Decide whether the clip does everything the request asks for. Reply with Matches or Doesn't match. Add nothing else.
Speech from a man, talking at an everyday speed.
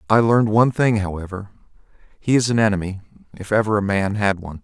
Matches